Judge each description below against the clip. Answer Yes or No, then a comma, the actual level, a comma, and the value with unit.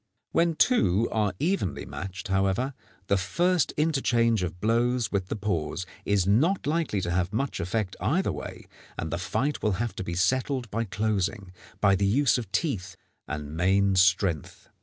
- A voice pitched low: Yes, low, 100 Hz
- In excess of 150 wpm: Yes, average, 165 wpm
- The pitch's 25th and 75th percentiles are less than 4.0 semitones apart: No, average, 5.2 semitones